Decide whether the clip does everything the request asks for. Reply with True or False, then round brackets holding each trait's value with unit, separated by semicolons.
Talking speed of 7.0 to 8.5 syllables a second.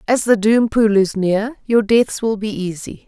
False (4.2 syllables/s)